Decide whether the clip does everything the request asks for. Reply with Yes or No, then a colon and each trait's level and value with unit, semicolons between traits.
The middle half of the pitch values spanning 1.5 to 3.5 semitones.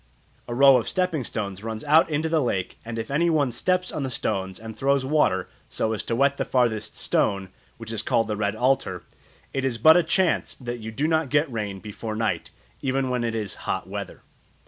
No: average, 4.7 semitones